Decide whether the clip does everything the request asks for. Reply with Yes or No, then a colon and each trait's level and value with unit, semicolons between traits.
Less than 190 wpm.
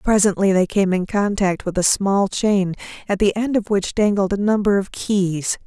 No: average, 200 wpm